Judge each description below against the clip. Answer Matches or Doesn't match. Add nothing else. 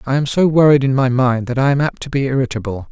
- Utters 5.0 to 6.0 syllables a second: Doesn't match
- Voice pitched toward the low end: Matches